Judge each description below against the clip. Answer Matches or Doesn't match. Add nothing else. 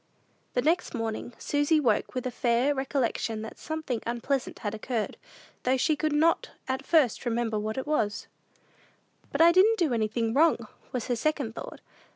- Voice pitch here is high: Matches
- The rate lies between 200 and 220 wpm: Doesn't match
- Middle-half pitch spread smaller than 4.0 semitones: Doesn't match